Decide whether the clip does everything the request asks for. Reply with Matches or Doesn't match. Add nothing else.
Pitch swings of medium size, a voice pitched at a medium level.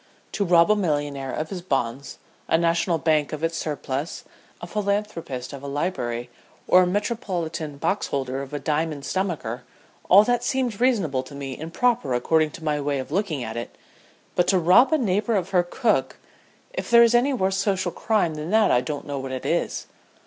Doesn't match